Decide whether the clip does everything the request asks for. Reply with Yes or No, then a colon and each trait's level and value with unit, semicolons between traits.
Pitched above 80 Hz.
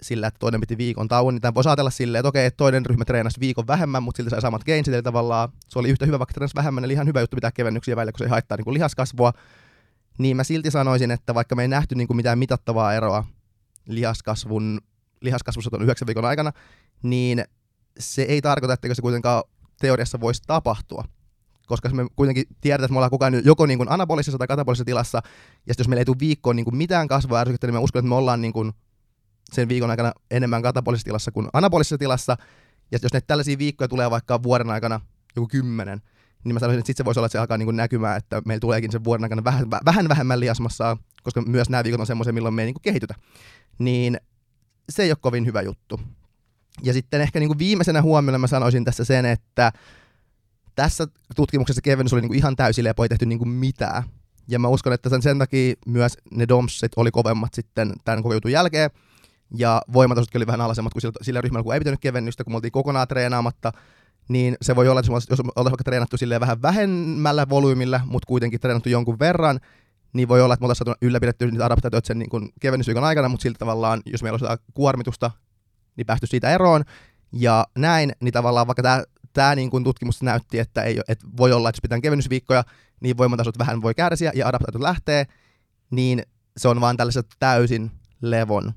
Yes: low, 120 Hz